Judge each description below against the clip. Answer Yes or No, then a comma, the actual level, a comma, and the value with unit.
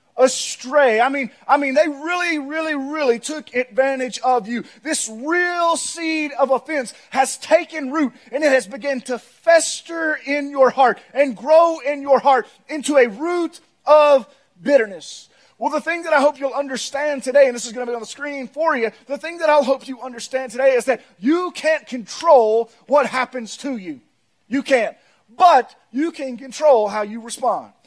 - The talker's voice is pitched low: No, very high, 275 Hz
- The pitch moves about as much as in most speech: Yes, average, 3.3 semitones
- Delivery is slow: No, average, 185 wpm